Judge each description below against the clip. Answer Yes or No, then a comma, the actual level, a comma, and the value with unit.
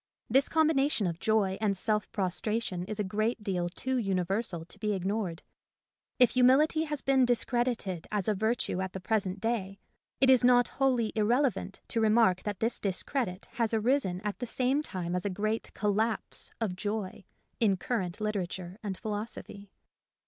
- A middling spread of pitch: Yes, average, 4.1 semitones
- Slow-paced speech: No, average, 165 wpm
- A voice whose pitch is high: Yes, high, 215 Hz